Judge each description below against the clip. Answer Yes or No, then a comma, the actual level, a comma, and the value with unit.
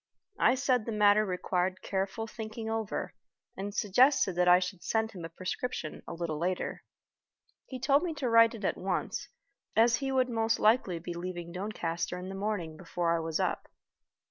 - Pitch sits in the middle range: No, high, 200 Hz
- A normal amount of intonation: Yes, average, 4.3 semitones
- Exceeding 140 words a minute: Yes, average, 180 wpm